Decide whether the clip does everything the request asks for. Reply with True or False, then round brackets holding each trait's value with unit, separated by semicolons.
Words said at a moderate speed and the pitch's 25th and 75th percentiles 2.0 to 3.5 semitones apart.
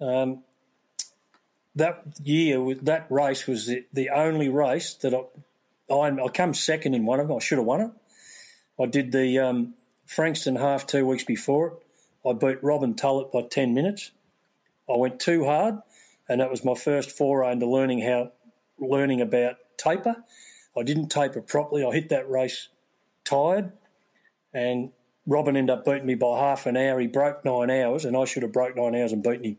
True (180 wpm; 2.8 semitones)